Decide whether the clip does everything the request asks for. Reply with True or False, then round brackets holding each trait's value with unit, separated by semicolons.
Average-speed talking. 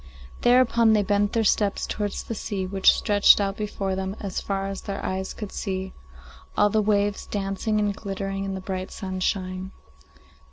True (170 wpm)